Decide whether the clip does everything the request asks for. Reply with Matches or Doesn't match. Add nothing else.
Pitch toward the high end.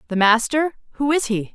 Matches